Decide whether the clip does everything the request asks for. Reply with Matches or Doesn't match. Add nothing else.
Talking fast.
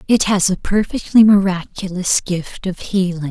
Doesn't match